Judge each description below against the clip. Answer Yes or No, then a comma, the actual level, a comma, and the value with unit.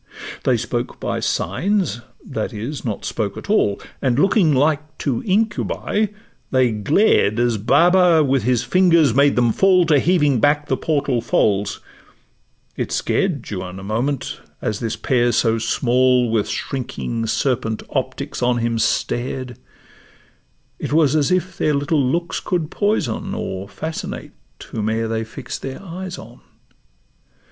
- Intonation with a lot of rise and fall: Yes, wide, 6.1 semitones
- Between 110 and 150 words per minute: Yes, average, 140 wpm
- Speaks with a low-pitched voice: Yes, low, 130 Hz